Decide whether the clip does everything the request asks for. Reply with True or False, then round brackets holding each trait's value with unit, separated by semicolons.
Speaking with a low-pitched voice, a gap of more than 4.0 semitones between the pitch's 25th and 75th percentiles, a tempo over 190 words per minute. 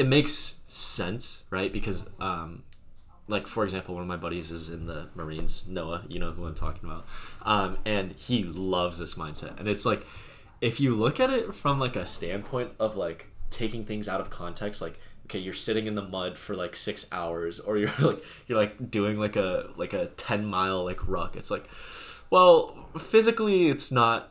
True (105 Hz; 4.6 semitones; 200 wpm)